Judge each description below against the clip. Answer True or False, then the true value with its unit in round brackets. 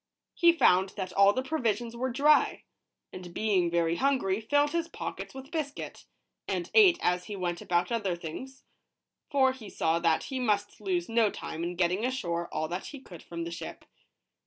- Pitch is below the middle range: False (200 Hz)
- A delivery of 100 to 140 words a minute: False (185 wpm)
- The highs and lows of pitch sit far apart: True (7.1 semitones)